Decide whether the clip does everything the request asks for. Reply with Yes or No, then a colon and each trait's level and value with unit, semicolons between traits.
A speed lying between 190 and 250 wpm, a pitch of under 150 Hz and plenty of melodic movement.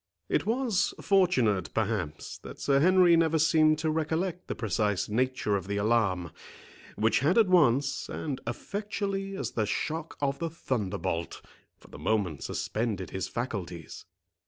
No: average, 145 wpm; low, 135 Hz; wide, 8.4 semitones